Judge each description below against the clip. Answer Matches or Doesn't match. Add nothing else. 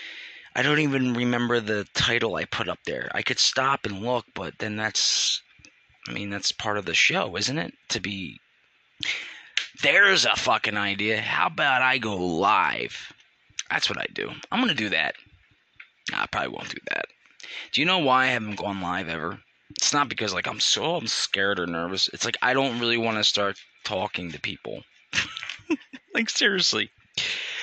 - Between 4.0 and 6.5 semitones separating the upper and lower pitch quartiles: Matches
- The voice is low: Matches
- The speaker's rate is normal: Matches